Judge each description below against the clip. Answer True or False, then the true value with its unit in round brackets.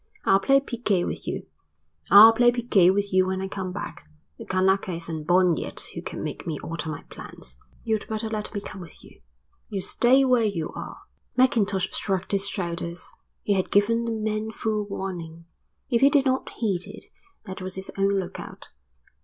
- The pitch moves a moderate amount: True (3.2 semitones)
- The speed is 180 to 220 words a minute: True (185 wpm)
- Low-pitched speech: False (195 Hz)